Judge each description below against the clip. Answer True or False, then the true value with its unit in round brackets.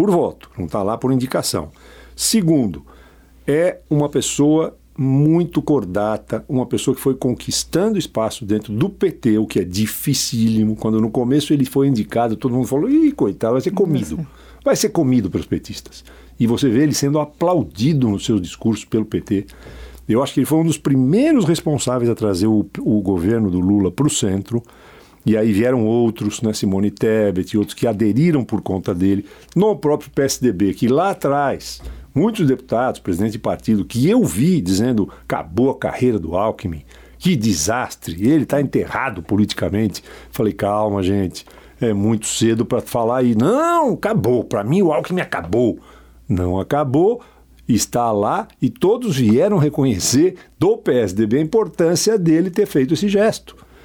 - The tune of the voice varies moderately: False (6.1 semitones)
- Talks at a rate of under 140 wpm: False (165 wpm)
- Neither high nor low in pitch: False (120 Hz)